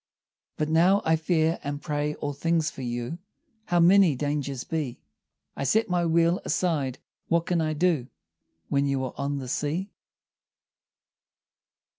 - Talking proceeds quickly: No, average, 145 wpm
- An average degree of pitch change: Yes, average, 3.2 semitones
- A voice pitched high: No, medium, 155 Hz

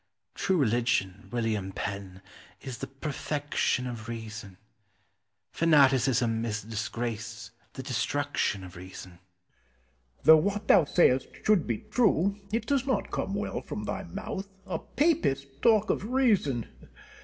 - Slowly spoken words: Yes, slow, 130 wpm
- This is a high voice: No, low, 135 Hz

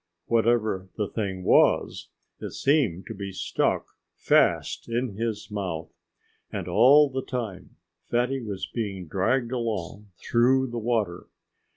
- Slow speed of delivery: Yes, slow, 130 wpm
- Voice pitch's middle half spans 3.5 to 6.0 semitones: Yes, average, 4.0 semitones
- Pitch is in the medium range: No, low, 115 Hz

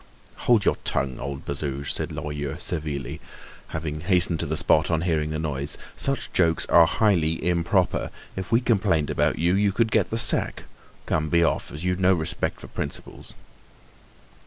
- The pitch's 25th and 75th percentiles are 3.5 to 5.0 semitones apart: Yes, average, 3.8 semitones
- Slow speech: No, average, 170 wpm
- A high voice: No, very low, 85 Hz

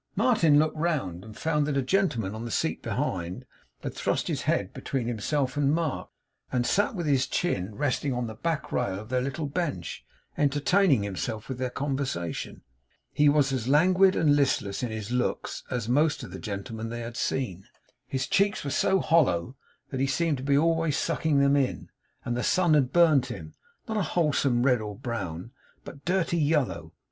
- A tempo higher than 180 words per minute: Yes, average, 190 wpm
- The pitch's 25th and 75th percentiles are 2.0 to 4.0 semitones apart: No, average, 4.8 semitones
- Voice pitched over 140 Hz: No, low, 135 Hz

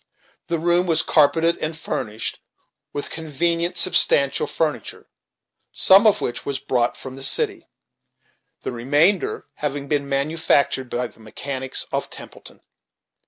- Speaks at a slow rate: Yes, slow, 125 wpm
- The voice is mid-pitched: Yes, medium, 145 Hz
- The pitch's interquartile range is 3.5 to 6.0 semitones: Yes, average, 4.0 semitones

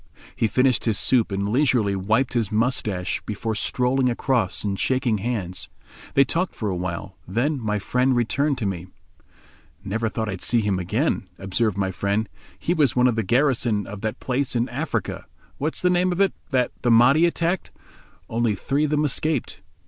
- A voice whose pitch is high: No, low, 120 Hz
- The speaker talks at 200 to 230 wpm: No, average, 175 wpm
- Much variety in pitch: No, average, 4.7 semitones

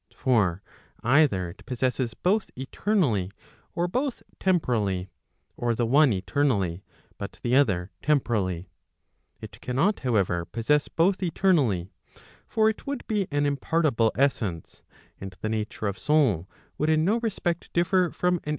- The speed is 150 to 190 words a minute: No, slow, 135 wpm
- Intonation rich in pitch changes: Yes, wide, 9.0 semitones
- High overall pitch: No, low, 130 Hz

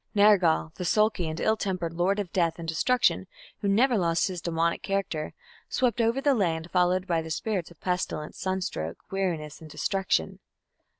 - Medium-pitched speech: Yes, medium, 180 Hz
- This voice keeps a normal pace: Yes, average, 170 wpm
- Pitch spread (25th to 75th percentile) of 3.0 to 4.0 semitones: Yes, average, 3.5 semitones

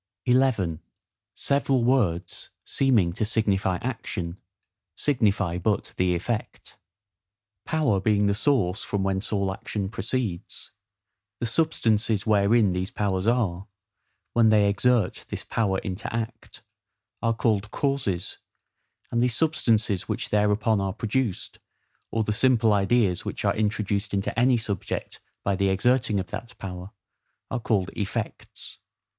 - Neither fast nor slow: No, slow, 130 wpm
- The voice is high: No, low, 105 Hz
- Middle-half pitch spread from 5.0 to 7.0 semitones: No, average, 3.4 semitones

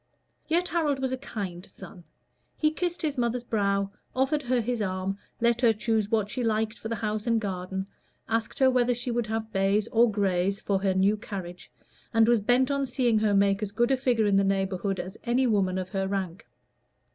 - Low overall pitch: No, high, 220 Hz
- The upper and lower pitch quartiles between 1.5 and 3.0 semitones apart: No, average, 3.7 semitones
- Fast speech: Yes, fast, 210 wpm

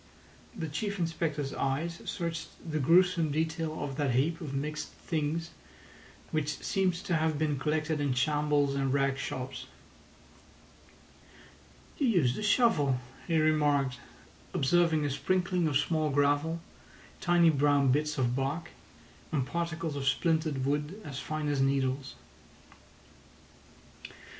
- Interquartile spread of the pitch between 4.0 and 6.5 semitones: No, average, 3.0 semitones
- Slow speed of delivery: Yes, slow, 125 wpm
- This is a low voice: No, medium, 150 Hz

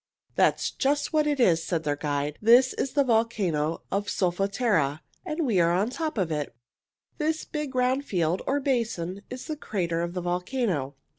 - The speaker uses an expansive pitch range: Yes, wide, 7.6 semitones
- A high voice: Yes, high, 200 Hz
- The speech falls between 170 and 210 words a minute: Yes, average, 180 wpm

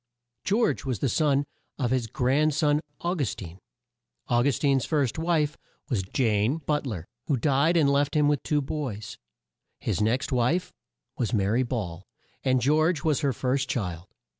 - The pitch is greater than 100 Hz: Yes, low, 135 Hz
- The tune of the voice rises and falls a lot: No, average, 4.3 semitones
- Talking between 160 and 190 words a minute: Yes, average, 170 wpm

